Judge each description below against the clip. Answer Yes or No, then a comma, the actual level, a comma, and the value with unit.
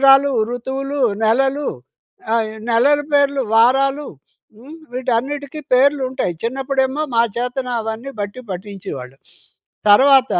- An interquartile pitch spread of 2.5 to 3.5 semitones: Yes, average, 3.1 semitones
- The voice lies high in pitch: Yes, very high, 265 Hz